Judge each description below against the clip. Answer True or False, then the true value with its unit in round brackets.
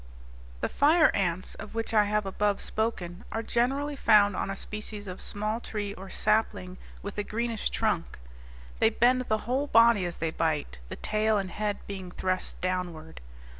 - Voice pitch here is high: True (210 Hz)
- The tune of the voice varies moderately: True (3.5 semitones)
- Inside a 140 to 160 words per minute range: False (170 wpm)